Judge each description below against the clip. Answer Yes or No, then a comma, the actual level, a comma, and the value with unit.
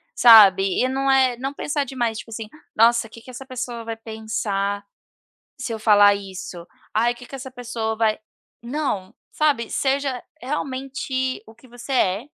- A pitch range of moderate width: Yes, average, 3.1 semitones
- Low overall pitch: No, high, 235 Hz